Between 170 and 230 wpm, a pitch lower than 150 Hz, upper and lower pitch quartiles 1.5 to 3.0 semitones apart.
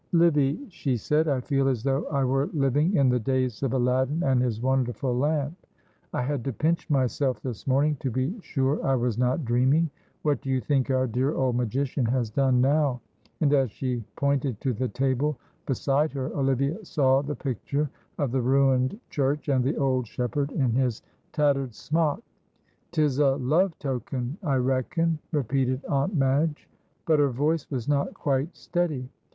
Yes: average, 175 wpm; low, 135 Hz; narrow, 2.4 semitones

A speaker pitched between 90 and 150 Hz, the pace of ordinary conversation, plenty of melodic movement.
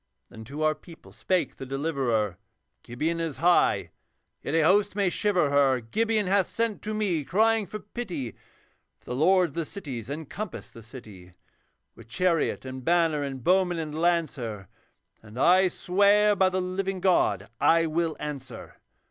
No: medium, 165 Hz; average, 160 wpm; wide, 6.0 semitones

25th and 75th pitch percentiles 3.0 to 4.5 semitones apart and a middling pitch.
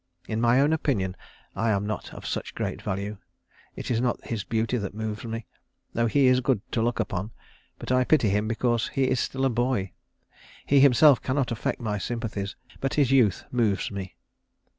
No: average, 3.4 semitones; low, 115 Hz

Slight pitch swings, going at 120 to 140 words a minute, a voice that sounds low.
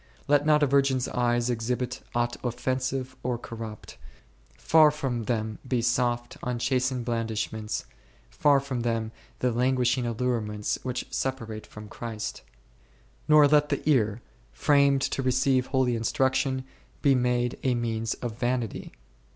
Yes: narrow, 2.2 semitones; slow, 135 wpm; low, 125 Hz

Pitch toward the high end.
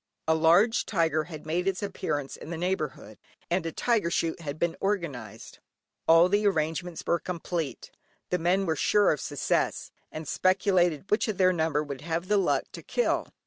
No: medium, 170 Hz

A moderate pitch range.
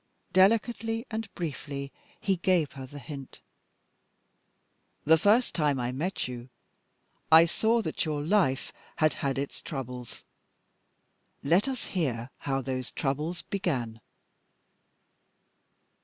No: wide, 6.0 semitones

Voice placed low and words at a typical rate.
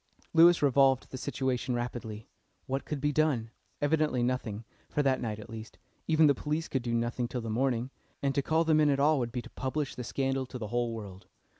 No: low, 130 Hz; fast, 215 wpm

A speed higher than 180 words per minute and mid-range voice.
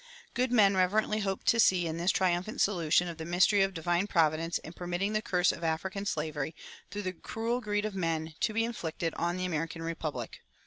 Yes: average, 200 wpm; medium, 180 Hz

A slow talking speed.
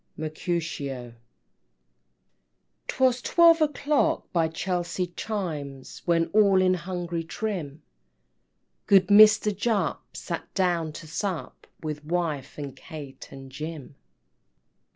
Yes: slow, 105 wpm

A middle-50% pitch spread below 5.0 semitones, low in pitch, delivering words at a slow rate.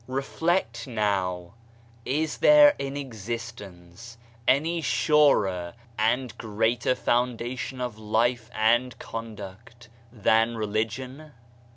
Yes: average, 3.1 semitones; low, 115 Hz; slow, 90 wpm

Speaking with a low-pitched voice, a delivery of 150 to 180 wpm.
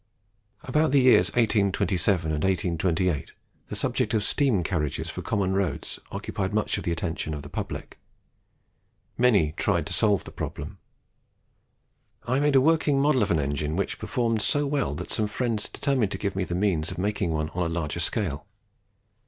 Yes: low, 100 Hz; average, 175 wpm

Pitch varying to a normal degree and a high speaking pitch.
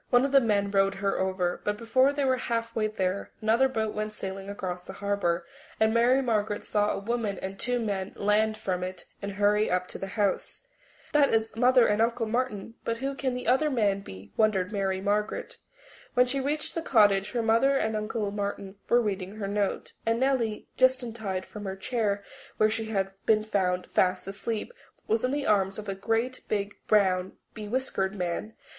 Yes: average, 3.1 semitones; high, 215 Hz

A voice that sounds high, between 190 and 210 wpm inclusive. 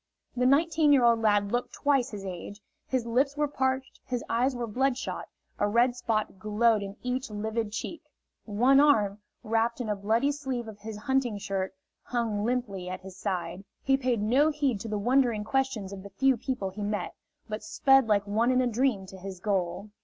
Yes: high, 230 Hz; average, 195 wpm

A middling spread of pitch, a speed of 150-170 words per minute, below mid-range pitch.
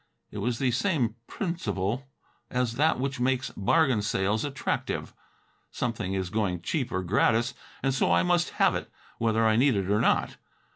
Yes: average, 4.6 semitones; average, 165 wpm; low, 115 Hz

